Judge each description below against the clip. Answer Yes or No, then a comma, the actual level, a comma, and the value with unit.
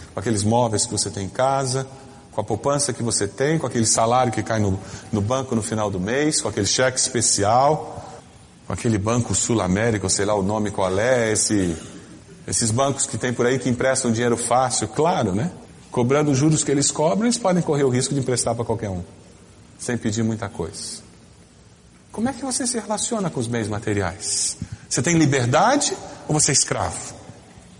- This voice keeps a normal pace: No, fast, 190 wpm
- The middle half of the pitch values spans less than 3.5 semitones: No, average, 4.8 semitones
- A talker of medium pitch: No, low, 120 Hz